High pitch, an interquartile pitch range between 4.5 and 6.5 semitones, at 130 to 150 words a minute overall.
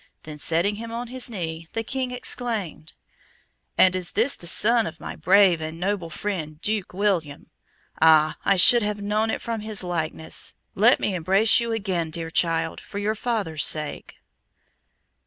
No: high, 195 Hz; average, 5.3 semitones; average, 165 wpm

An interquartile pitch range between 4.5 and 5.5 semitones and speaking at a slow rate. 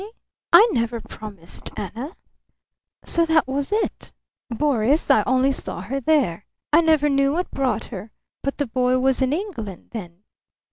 No: average, 5.0 semitones; average, 155 wpm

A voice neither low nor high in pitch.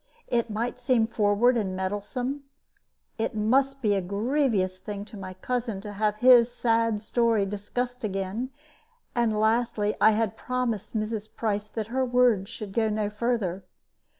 No: high, 220 Hz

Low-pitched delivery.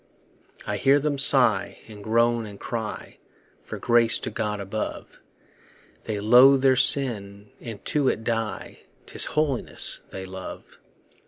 Yes: low, 115 Hz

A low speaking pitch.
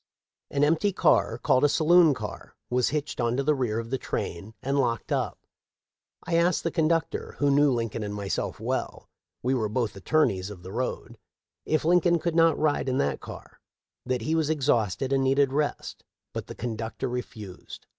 Yes: low, 130 Hz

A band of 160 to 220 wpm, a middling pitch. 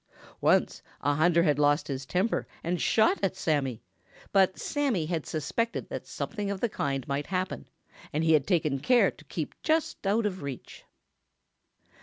Yes: average, 165 wpm; medium, 170 Hz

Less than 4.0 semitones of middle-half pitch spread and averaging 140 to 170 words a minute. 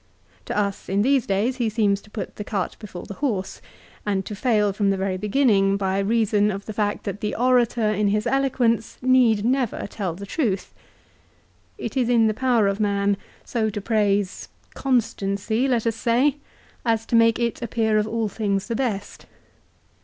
No: average, 2.9 semitones; average, 185 wpm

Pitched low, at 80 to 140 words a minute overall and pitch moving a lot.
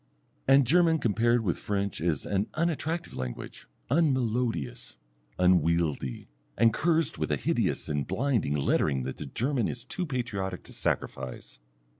Yes: low, 110 Hz; slow, 135 wpm; wide, 8.9 semitones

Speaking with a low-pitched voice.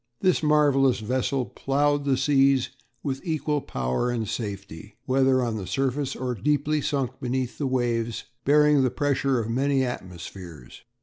Yes: low, 130 Hz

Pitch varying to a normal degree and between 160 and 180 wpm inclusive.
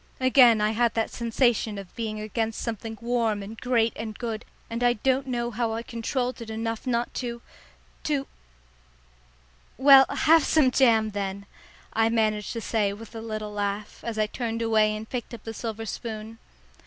No: narrow, 1.9 semitones; average, 175 wpm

